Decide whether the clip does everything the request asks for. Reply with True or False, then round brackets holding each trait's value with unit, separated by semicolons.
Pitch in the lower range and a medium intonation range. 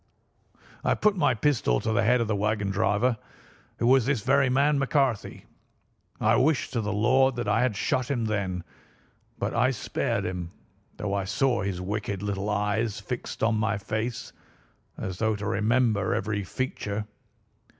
True (110 Hz; 3.8 semitones)